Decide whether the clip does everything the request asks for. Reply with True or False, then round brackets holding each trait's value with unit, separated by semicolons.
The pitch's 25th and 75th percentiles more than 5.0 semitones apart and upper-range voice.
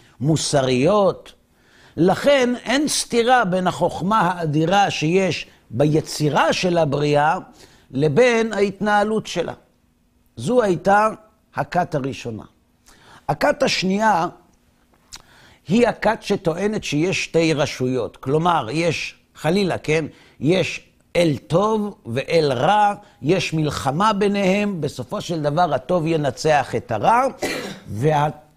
False (5.6 semitones; 165 Hz)